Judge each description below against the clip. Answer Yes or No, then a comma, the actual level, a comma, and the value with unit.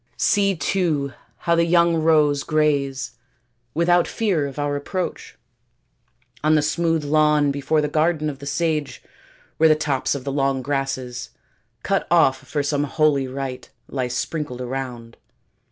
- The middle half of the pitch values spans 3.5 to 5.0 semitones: No, average, 2.8 semitones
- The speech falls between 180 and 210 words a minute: No, average, 145 wpm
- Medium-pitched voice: Yes, medium, 145 Hz